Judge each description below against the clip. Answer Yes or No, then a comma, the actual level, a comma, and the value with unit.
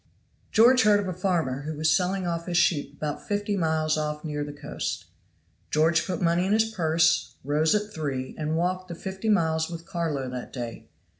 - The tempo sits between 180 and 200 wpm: Yes, average, 195 wpm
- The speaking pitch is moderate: Yes, medium, 165 Hz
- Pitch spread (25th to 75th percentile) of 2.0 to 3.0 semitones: No, average, 3.7 semitones